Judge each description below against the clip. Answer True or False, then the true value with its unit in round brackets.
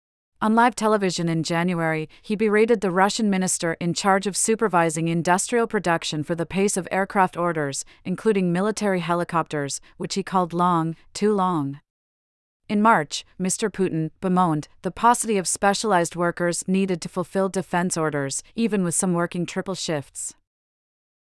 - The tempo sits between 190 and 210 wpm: False (145 wpm)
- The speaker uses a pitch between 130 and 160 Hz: False (180 Hz)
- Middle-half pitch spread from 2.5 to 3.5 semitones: True (3.2 semitones)